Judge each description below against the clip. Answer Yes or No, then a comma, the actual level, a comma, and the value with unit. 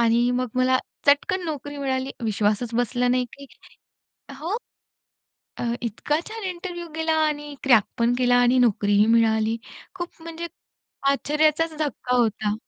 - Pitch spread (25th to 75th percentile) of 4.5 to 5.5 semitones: Yes, average, 4.8 semitones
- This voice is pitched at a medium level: No, very high, 260 Hz